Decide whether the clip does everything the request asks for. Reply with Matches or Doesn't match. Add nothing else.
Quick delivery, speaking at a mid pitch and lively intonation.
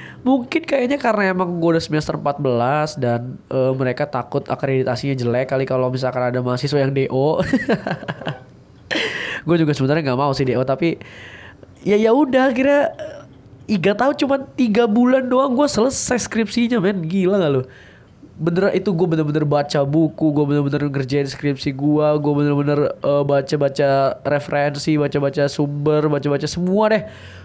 Matches